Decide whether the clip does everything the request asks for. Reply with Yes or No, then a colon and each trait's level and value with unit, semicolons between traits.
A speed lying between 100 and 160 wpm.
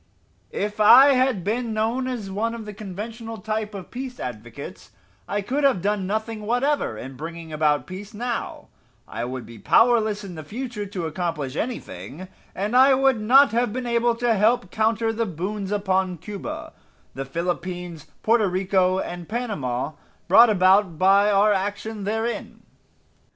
Yes: average, 155 wpm